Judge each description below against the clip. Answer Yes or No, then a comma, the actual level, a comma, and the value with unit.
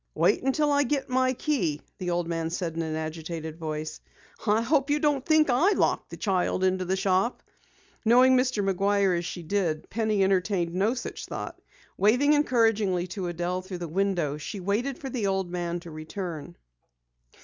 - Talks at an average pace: Yes, average, 180 wpm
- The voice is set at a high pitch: Yes, high, 195 Hz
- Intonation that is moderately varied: No, wide, 6.1 semitones